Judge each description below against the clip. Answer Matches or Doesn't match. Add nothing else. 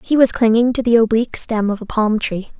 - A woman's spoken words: Matches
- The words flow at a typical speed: Doesn't match